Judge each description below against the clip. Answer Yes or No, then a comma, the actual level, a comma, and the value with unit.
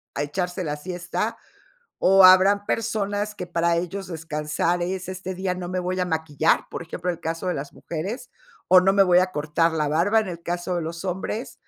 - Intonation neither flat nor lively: No, narrow, 2.3 semitones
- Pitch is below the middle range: No, medium, 180 Hz